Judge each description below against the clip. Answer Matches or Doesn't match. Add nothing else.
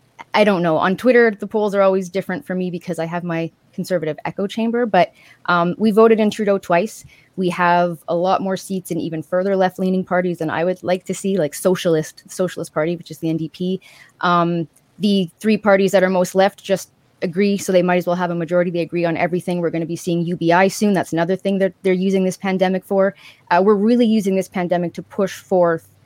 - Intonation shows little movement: Matches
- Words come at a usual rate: Doesn't match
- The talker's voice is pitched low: Doesn't match